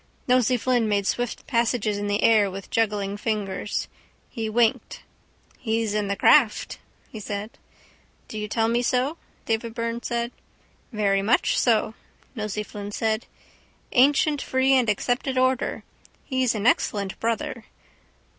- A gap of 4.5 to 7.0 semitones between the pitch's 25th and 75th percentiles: No, average, 2.8 semitones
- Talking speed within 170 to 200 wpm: No, slow, 135 wpm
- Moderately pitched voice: No, high, 225 Hz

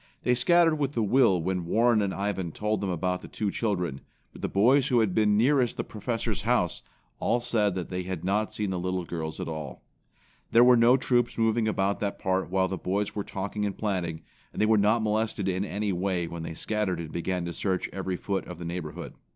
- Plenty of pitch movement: No, average, 3.5 semitones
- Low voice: Yes, low, 100 Hz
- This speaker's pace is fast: Yes, fast, 225 wpm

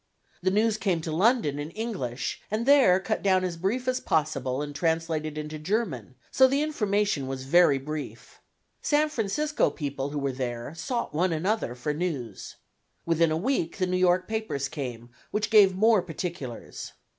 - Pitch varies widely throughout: Yes, wide, 6.7 semitones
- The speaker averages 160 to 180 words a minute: Yes, average, 170 wpm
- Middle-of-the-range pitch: Yes, medium, 175 Hz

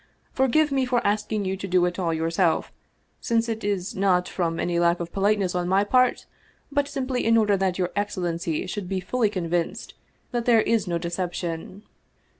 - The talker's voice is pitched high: Yes, high, 195 Hz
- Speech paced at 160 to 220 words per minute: Yes, average, 190 wpm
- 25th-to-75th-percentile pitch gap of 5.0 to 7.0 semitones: No, average, 4.4 semitones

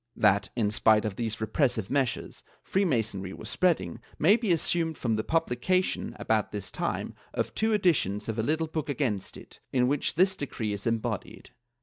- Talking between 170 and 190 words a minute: Yes, average, 180 wpm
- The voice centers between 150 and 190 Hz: No, low, 125 Hz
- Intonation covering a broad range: Yes, wide, 7.1 semitones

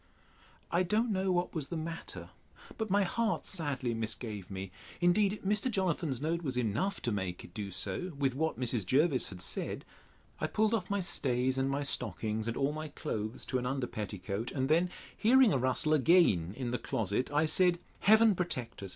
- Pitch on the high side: No, medium, 140 Hz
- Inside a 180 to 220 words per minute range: Yes, average, 190 wpm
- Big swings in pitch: Yes, wide, 7.7 semitones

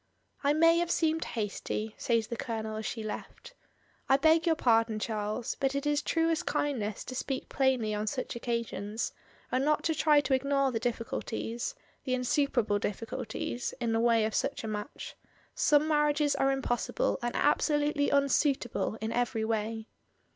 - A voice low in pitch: No, very high, 250 Hz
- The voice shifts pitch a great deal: No, average, 4.6 semitones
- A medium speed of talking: Yes, average, 170 wpm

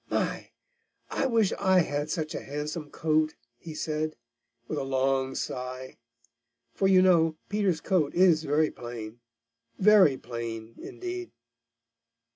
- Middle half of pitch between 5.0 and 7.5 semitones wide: Yes, wide, 5.6 semitones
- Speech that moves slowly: Yes, slow, 125 wpm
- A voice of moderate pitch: Yes, medium, 155 Hz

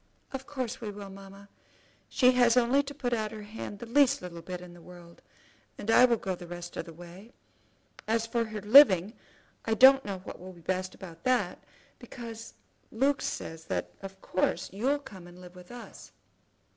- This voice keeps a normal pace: Yes, average, 195 wpm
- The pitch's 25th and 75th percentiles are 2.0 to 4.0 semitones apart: No, average, 5.2 semitones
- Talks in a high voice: Yes, high, 210 Hz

